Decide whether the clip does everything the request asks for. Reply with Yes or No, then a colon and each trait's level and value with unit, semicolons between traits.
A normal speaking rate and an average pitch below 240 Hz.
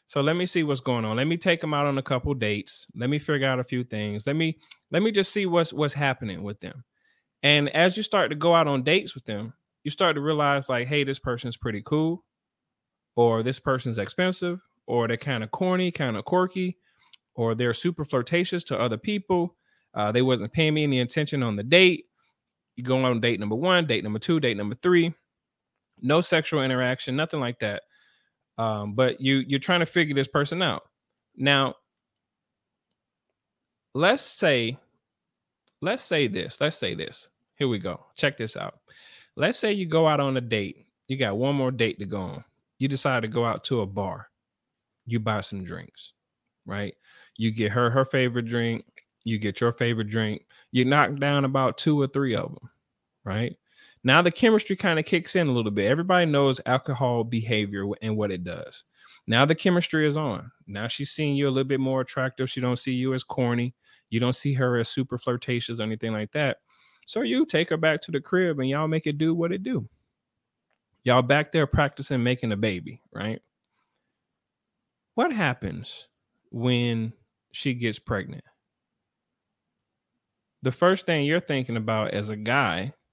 Yes: average, 190 wpm; low, 135 Hz